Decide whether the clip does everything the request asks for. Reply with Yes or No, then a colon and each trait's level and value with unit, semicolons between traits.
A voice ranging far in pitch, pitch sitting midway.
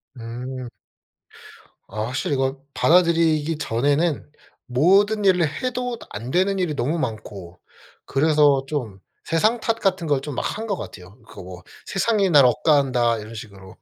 Yes: wide, 7.1 semitones; medium, 145 Hz